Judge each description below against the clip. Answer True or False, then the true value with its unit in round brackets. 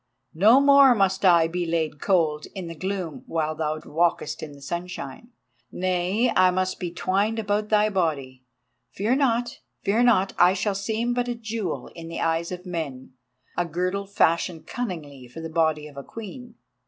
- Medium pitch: True (180 Hz)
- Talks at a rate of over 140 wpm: True (170 wpm)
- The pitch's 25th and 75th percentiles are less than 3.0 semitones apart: False (4.6 semitones)